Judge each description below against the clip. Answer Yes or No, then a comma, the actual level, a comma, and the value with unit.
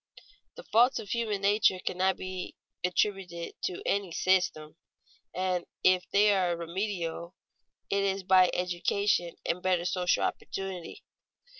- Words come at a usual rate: No, slow, 125 wpm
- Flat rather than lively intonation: Yes, narrow, 2.0 semitones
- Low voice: No, medium, 185 Hz